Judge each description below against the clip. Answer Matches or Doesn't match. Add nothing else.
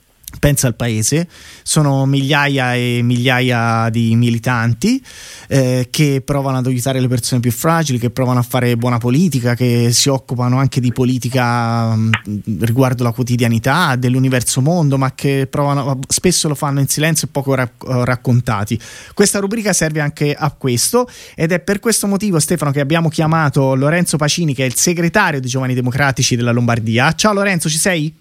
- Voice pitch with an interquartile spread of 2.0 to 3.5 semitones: Doesn't match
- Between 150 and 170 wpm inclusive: Matches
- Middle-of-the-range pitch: Doesn't match